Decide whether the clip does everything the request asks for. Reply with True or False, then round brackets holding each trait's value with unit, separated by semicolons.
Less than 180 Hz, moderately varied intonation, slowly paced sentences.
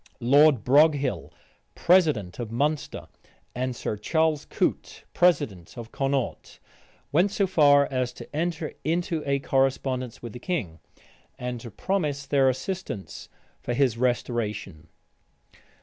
True (135 Hz; 4.4 semitones; 120 wpm)